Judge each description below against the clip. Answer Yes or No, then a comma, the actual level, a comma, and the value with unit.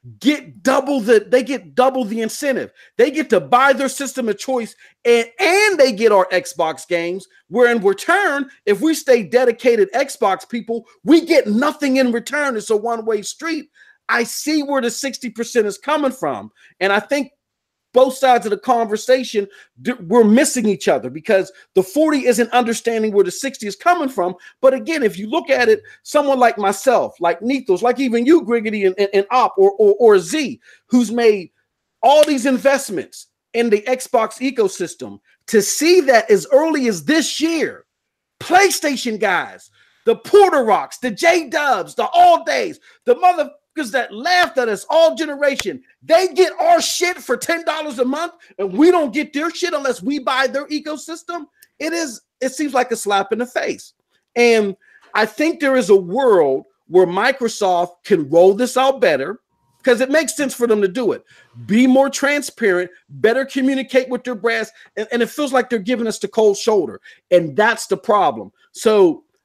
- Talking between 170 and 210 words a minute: Yes, average, 185 wpm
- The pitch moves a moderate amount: No, wide, 5.8 semitones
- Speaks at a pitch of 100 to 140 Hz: No, very high, 255 Hz